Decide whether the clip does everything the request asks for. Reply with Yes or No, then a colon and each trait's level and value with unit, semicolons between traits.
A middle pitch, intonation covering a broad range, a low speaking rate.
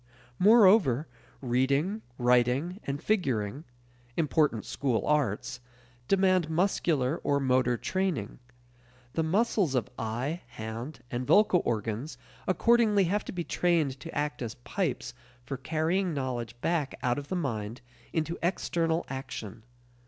Yes: medium, 145 Hz; wide, 6.1 semitones; slow, 125 wpm